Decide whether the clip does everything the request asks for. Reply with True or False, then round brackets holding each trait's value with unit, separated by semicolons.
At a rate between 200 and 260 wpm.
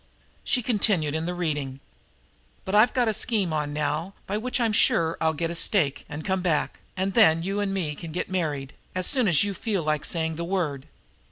True (205 wpm)